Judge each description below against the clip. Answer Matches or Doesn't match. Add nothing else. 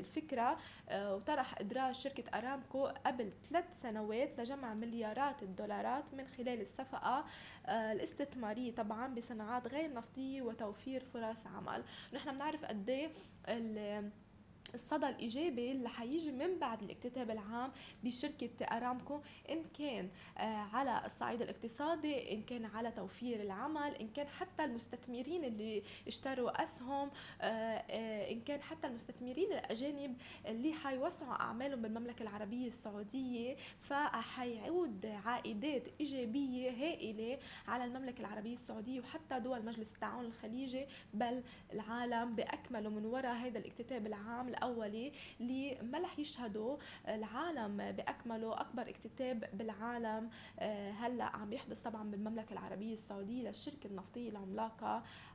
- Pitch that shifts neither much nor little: Matches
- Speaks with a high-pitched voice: Matches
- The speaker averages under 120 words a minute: Matches